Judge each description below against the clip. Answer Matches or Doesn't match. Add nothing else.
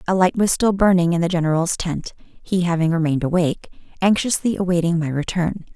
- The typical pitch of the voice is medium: Matches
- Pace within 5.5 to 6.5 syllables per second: Matches